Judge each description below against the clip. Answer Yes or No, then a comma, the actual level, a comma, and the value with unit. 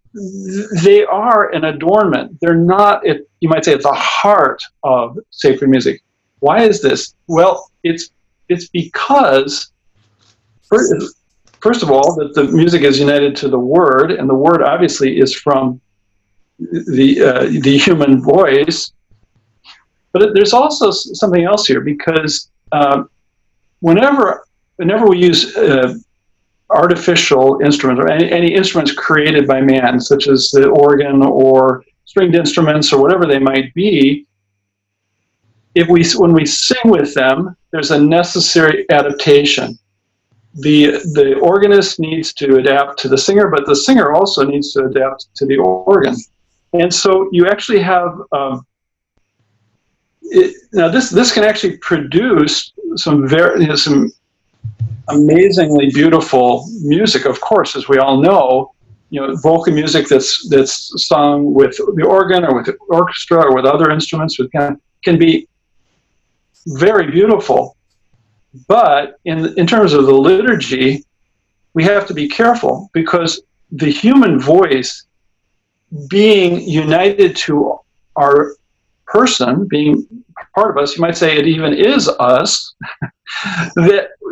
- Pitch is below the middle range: No, medium, 150 Hz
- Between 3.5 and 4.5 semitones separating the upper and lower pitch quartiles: No, average, 5.2 semitones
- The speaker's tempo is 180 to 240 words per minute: No, slow, 135 wpm